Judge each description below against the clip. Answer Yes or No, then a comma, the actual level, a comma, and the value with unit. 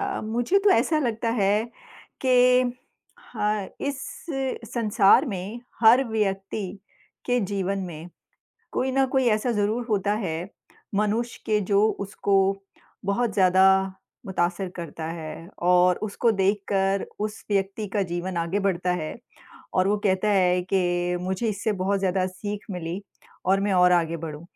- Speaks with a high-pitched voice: Yes, high, 195 Hz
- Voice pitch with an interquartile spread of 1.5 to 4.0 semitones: Yes, average, 3.2 semitones